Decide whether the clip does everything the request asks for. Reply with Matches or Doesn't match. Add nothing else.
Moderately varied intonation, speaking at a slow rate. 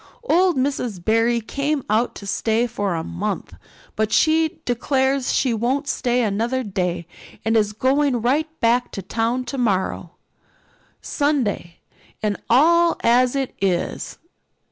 Matches